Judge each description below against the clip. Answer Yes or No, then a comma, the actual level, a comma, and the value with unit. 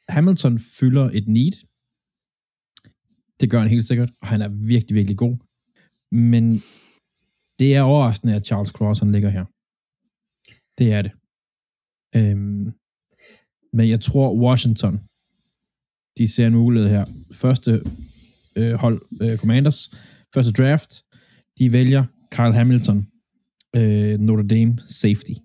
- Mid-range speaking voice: No, low, 115 Hz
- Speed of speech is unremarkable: No, slow, 125 wpm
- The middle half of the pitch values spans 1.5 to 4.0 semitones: Yes, average, 3.2 semitones